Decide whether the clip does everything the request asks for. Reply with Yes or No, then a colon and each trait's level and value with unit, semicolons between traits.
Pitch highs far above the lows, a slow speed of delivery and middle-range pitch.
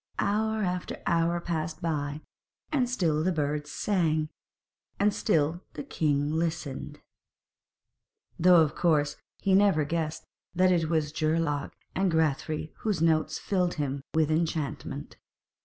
No: average, 2.8 semitones; slow, 125 wpm; medium, 160 Hz